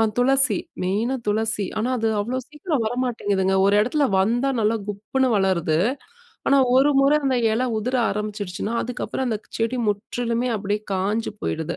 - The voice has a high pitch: Yes, high, 225 Hz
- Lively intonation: No, average, 3.8 semitones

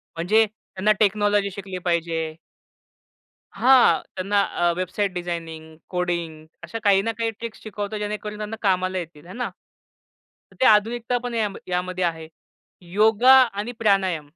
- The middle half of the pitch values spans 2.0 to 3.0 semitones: No, average, 3.5 semitones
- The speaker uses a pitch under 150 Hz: No, high, 195 Hz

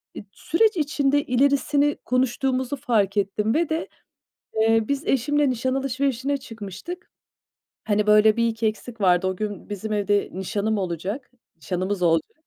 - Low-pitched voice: No, high, 230 Hz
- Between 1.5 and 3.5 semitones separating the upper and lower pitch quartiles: No, average, 5.3 semitones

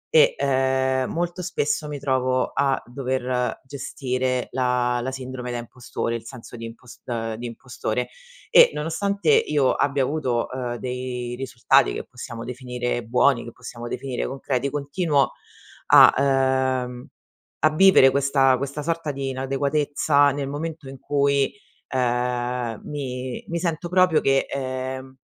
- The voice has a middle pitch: No, low, 130 Hz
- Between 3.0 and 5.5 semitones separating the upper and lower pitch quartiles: No, narrow, 2.4 semitones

